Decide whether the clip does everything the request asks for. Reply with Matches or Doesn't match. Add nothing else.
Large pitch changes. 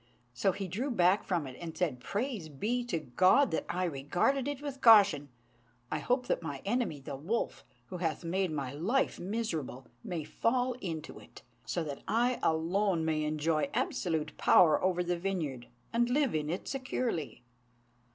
Matches